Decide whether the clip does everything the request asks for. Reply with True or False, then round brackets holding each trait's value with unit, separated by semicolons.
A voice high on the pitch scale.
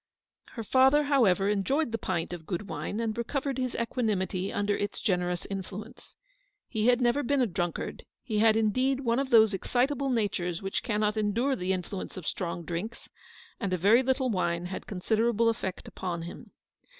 True (215 Hz)